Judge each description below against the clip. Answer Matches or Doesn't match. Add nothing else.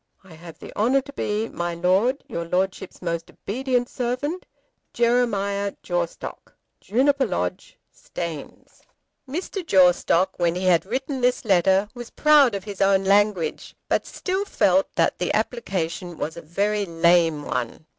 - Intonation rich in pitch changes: Matches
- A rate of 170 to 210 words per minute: Doesn't match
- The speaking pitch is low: Doesn't match